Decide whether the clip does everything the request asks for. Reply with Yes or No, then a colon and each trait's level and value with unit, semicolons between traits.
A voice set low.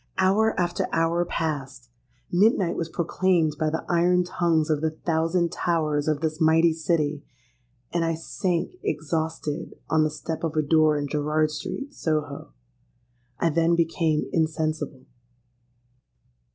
No: medium, 160 Hz